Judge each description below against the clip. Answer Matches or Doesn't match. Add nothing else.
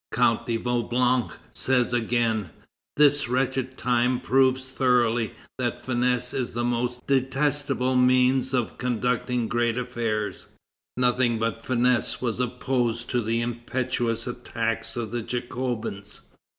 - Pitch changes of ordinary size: Doesn't match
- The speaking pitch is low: Matches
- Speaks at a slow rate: Matches